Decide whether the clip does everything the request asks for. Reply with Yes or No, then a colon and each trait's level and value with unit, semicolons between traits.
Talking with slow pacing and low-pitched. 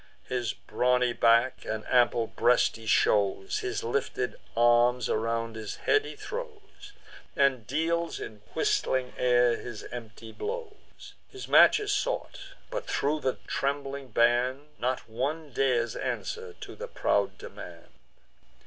Yes: slow, 130 wpm; low, 130 Hz